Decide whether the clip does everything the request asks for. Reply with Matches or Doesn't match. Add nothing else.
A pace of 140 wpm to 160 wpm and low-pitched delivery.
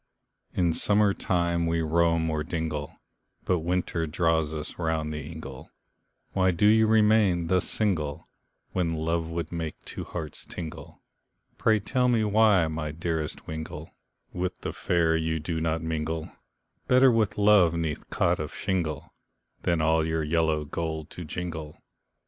Matches